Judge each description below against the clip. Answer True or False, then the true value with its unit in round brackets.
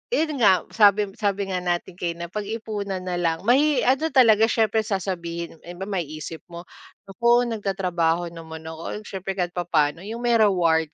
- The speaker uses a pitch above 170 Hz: True (190 Hz)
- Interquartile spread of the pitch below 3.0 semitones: False (4.1 semitones)